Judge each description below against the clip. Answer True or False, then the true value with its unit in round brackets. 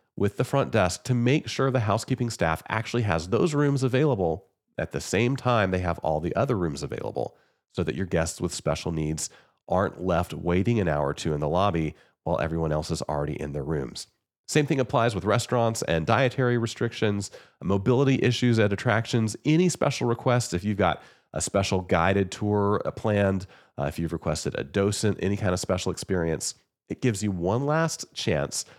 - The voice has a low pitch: True (100 Hz)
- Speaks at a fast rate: False (190 wpm)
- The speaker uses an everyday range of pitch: False (6.2 semitones)